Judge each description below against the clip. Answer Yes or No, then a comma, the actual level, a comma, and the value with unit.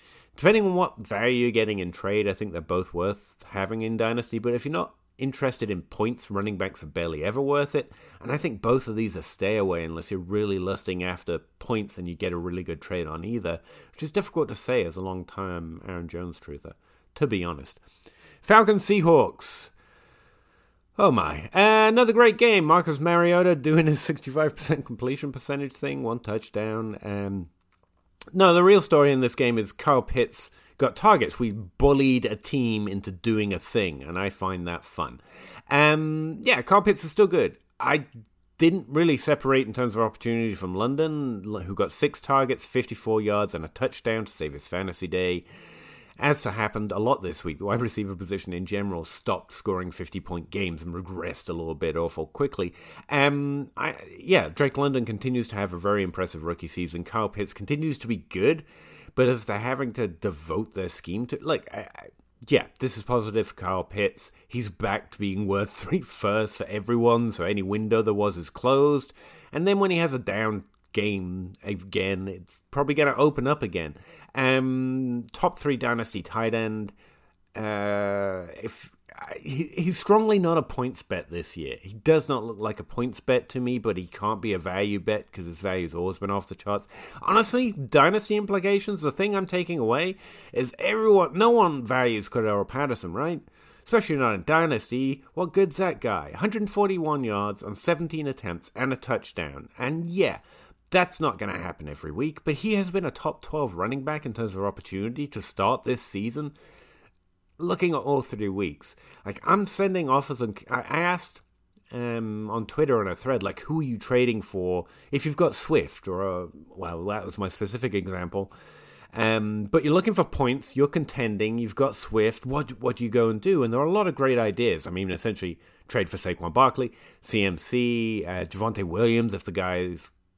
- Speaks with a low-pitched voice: Yes, low, 115 Hz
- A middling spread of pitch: No, wide, 6.9 semitones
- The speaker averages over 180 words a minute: Yes, average, 190 wpm